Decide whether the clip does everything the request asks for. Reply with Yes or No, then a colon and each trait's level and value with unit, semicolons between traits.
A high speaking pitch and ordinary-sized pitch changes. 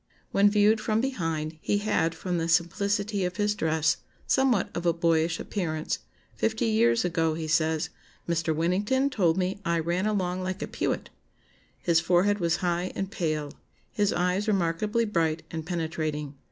No: medium, 175 Hz; average, 3.9 semitones